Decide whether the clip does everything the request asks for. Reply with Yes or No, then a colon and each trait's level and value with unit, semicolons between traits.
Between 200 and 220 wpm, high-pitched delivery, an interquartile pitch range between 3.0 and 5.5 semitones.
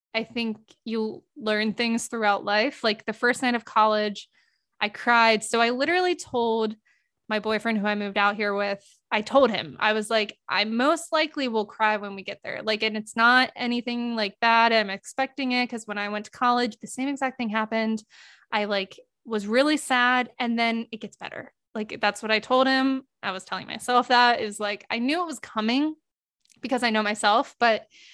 No: fast, 205 wpm; high, 225 Hz; narrow, 2.5 semitones